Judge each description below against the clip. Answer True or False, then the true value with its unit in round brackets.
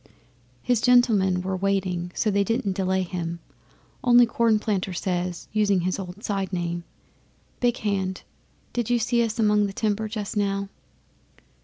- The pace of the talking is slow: False (150 wpm)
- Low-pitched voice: False (200 Hz)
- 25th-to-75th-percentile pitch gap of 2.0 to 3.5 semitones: True (2.9 semitones)